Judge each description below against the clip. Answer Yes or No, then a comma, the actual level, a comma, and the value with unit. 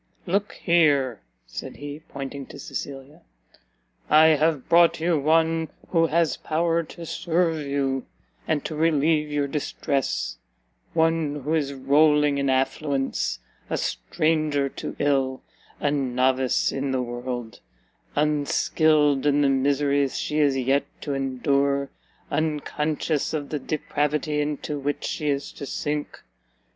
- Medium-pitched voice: Yes, medium, 145 Hz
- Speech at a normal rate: No, slow, 130 wpm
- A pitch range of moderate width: No, narrow, 2.2 semitones